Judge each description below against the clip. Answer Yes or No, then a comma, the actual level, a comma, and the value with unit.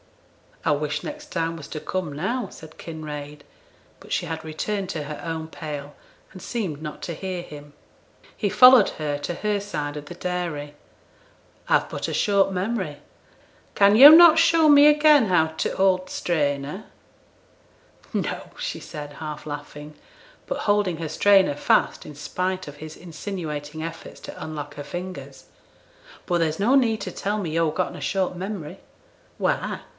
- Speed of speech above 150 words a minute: Yes, average, 165 wpm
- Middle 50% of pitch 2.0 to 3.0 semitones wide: No, average, 4.9 semitones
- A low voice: No, medium, 170 Hz